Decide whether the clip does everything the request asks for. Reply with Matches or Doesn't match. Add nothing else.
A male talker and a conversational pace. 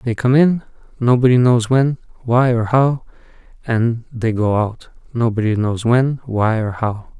Matches